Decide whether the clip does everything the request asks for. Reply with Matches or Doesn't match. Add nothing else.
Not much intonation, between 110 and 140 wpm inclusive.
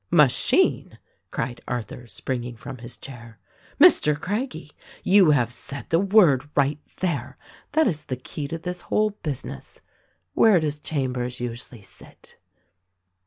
Doesn't match